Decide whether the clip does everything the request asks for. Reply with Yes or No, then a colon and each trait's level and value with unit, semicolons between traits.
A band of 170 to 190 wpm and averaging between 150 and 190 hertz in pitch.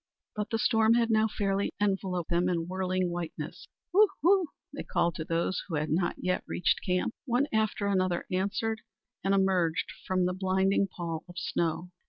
Yes: average, 175 wpm; medium, 185 Hz